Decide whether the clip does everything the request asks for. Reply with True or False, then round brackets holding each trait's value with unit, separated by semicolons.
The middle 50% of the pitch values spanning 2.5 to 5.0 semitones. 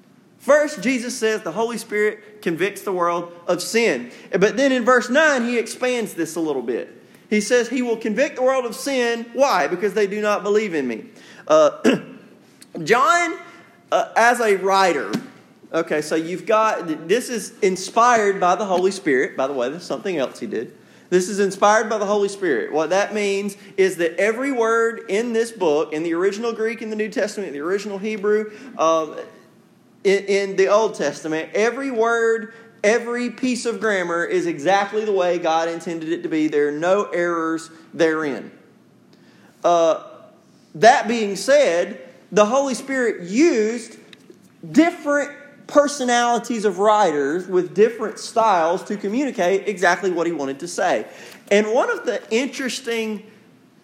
True (4.5 semitones)